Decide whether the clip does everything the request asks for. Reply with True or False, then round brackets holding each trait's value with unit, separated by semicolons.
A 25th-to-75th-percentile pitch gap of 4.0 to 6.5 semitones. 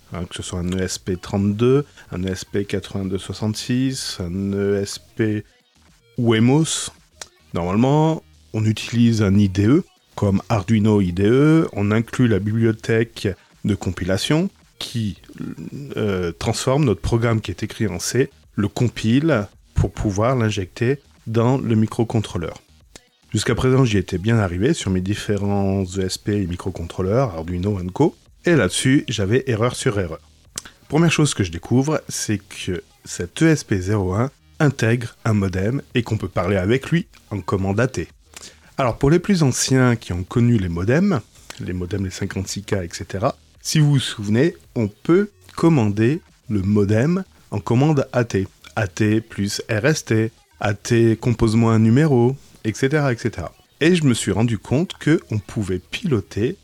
True (4.3 semitones)